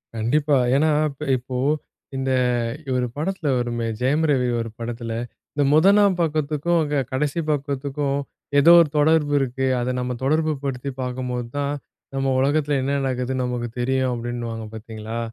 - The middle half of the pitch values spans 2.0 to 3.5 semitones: Yes, average, 3.2 semitones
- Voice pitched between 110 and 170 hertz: Yes, low, 135 Hz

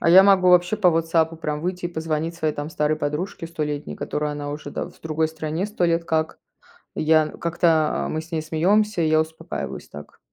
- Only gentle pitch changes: Yes, narrow, 1.9 semitones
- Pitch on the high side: No, medium, 160 Hz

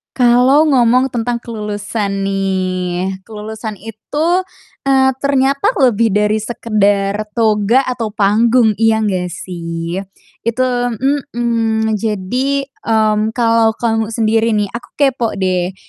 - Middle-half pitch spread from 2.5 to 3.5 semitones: Yes, average, 2.9 semitones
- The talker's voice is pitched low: No, high, 220 Hz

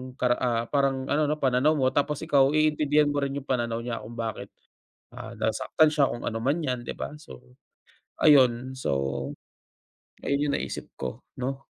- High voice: No, low, 135 Hz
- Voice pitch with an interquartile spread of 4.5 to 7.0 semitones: No, average, 3.3 semitones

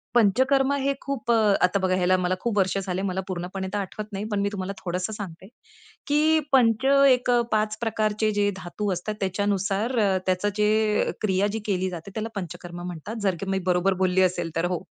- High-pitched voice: Yes, high, 200 Hz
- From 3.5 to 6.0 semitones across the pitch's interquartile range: No, average, 2.8 semitones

